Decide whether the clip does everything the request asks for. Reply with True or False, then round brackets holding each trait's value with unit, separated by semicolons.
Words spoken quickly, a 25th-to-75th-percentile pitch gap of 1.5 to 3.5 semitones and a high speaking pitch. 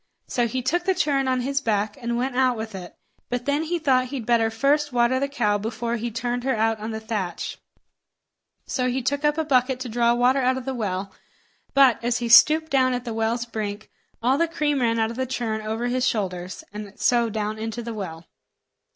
True (220 wpm; 3.0 semitones; 240 Hz)